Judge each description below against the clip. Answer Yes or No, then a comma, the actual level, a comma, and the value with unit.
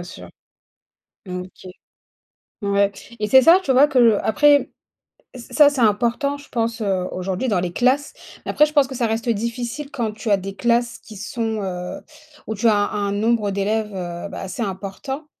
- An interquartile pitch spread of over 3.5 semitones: Yes, average, 4.2 semitones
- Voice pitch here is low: No, high, 220 Hz